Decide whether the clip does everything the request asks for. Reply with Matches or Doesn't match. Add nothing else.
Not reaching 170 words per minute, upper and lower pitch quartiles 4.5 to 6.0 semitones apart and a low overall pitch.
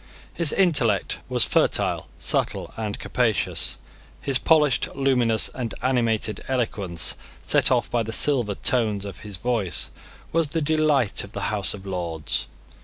Matches